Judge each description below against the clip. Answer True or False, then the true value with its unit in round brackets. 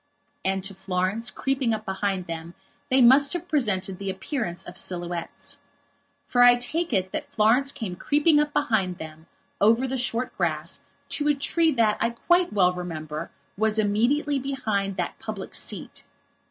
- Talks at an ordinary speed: True (160 wpm)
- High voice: True (215 Hz)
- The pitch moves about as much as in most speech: False (6.4 semitones)